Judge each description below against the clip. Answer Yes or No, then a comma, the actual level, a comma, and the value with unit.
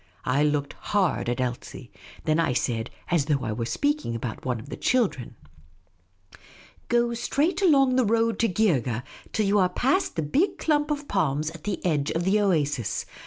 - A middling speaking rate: Yes, average, 185 wpm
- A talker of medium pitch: Yes, medium, 170 Hz